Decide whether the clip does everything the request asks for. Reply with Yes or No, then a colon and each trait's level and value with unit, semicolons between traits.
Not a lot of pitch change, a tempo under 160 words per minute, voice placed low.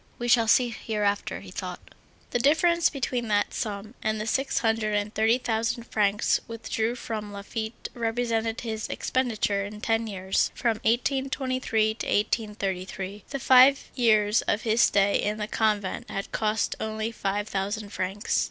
No: narrow, 2.3 semitones; average, 150 wpm; high, 220 Hz